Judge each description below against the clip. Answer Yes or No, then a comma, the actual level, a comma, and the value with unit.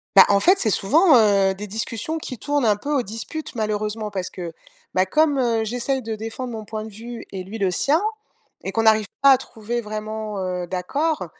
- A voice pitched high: Yes, high, 220 Hz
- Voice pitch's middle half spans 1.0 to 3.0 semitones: No, average, 3.8 semitones